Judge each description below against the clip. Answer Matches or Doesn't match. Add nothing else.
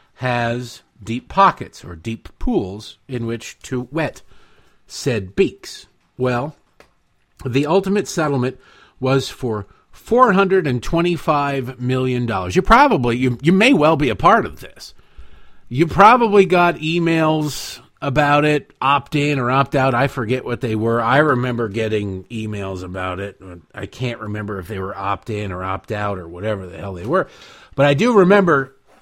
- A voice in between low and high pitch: Doesn't match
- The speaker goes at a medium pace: Matches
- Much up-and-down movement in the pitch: Matches